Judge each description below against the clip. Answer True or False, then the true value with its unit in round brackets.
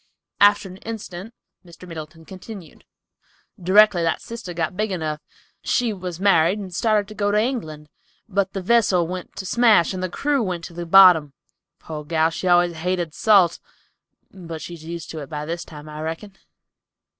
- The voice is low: False (180 Hz)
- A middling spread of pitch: True (3.7 semitones)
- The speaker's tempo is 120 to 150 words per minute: False (175 wpm)